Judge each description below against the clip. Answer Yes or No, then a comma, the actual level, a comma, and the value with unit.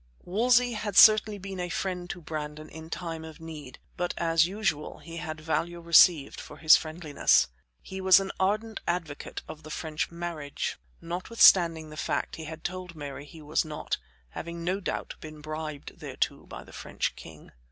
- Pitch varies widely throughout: No, average, 2.9 semitones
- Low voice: No, medium, 165 Hz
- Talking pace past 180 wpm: No, average, 175 wpm